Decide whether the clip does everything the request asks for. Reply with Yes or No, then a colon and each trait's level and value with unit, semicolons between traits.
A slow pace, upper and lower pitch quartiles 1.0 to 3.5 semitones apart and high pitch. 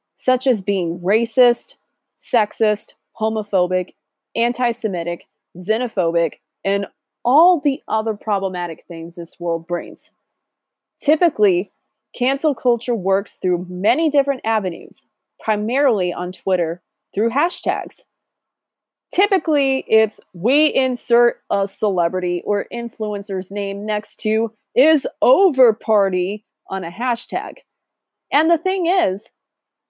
No: slow, 105 wpm; wide, 5.4 semitones; high, 220 Hz